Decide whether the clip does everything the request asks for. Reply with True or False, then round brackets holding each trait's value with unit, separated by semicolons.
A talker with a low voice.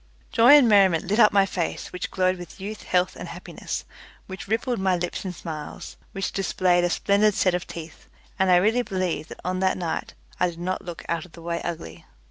False (185 Hz)